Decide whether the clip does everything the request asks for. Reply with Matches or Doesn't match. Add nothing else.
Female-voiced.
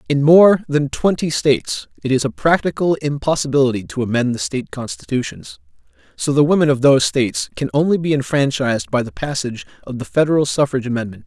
Doesn't match